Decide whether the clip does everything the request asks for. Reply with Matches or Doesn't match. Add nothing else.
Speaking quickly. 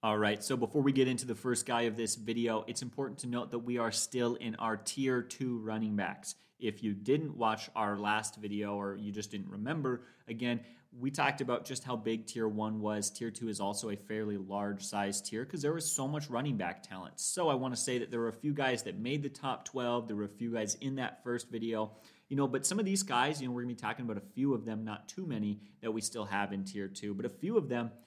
Matches